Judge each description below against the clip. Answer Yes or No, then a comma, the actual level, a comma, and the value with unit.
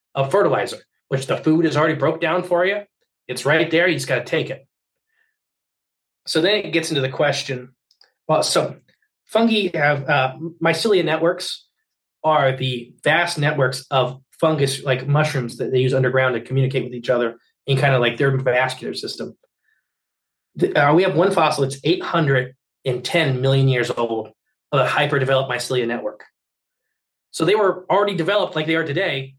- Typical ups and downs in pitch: Yes, average, 4.4 semitones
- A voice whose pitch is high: No, medium, 140 Hz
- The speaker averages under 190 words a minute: Yes, average, 170 wpm